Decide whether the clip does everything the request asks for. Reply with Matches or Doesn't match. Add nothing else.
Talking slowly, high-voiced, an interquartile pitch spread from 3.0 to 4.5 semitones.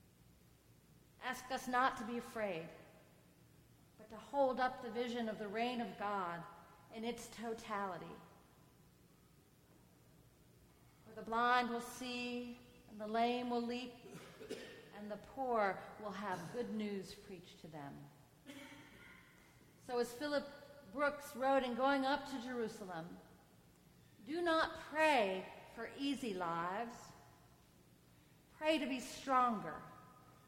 Doesn't match